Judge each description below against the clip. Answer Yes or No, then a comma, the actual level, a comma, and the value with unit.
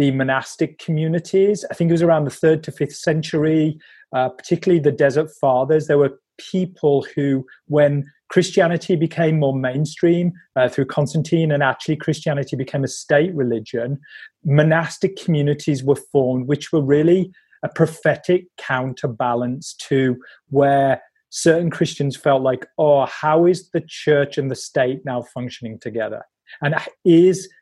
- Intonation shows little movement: No, average, 3.4 semitones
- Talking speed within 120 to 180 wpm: Yes, average, 145 wpm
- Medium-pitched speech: Yes, medium, 150 Hz